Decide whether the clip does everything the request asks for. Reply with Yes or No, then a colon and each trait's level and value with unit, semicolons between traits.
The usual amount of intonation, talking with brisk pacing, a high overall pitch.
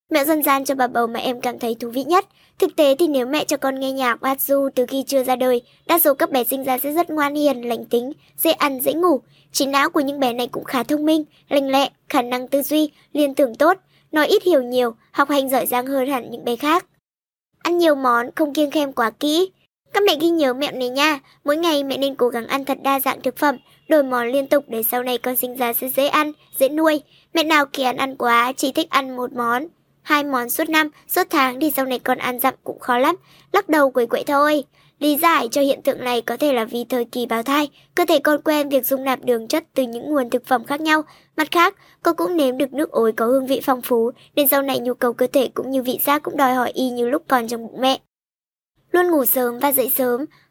Yes: average, 3.2 semitones; fast, 260 wpm; very high, 275 Hz